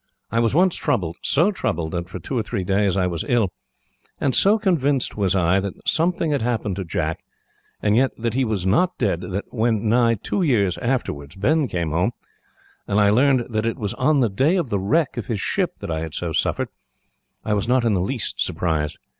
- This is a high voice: No, low, 110 Hz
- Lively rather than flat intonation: Yes, wide, 5.8 semitones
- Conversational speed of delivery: No, fast, 215 wpm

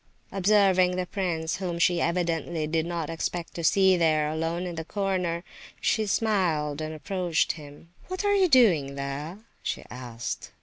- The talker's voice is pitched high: No, medium, 170 Hz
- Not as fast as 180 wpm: Yes, average, 160 wpm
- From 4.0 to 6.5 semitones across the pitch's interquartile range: No, average, 3.3 semitones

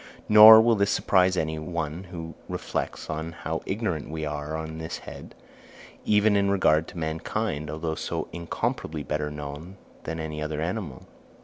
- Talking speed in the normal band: Yes, average, 150 wpm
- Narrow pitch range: No, average, 3.5 semitones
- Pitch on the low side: Yes, very low, 80 Hz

